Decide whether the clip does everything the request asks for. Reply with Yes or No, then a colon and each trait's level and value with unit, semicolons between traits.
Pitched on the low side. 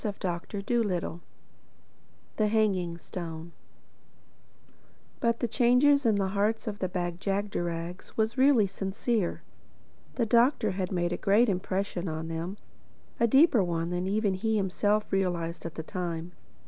No: high, 195 Hz